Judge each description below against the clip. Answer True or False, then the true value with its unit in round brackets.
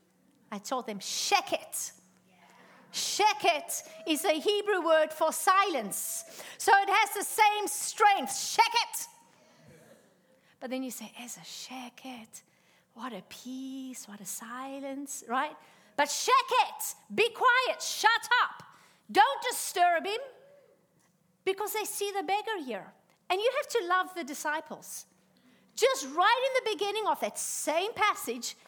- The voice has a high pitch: True (360 Hz)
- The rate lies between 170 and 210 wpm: False (140 wpm)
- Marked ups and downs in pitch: True (8.4 semitones)